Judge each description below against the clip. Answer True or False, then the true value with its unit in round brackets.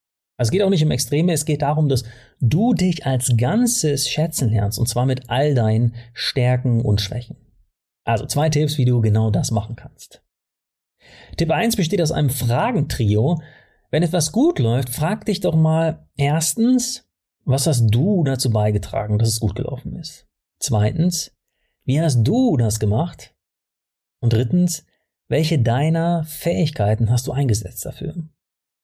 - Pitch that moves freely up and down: True (5.8 semitones)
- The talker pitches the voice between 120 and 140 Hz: True (135 Hz)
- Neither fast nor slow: True (155 wpm)